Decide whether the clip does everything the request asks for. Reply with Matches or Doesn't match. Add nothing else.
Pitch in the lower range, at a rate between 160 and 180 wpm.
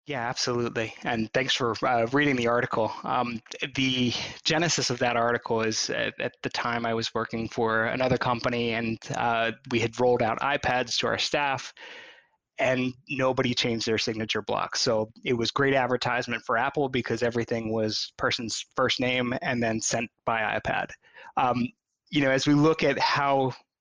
Matches